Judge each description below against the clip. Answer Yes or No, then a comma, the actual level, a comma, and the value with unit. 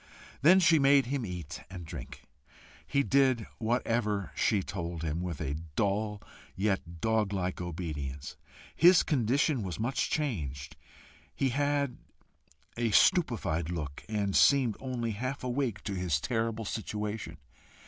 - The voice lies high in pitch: No, low, 105 Hz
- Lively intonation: Yes, wide, 6.5 semitones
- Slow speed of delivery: Yes, slow, 130 wpm